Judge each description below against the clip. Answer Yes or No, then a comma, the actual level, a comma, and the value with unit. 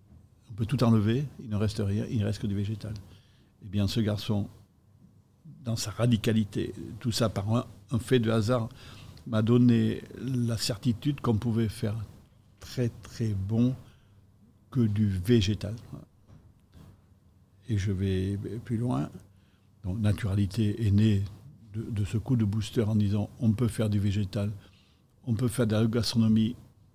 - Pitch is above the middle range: No, low, 110 Hz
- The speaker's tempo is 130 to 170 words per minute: Yes, average, 155 wpm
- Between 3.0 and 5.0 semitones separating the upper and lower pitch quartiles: No, narrow, 2.4 semitones